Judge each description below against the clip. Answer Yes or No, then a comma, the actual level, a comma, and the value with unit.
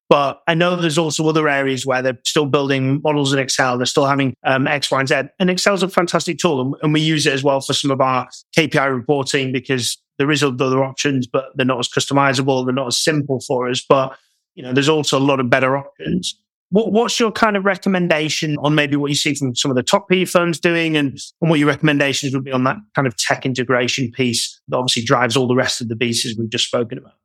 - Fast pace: Yes, fast, 245 wpm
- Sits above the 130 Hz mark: Yes, medium, 140 Hz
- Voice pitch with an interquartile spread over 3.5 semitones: No, average, 3.1 semitones